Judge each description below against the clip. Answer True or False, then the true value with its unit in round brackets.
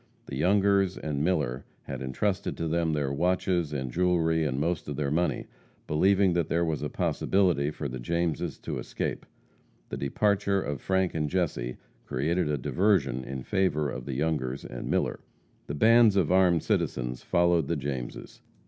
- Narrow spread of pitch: False (4.8 semitones)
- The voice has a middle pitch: False (80 Hz)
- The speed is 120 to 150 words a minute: False (165 wpm)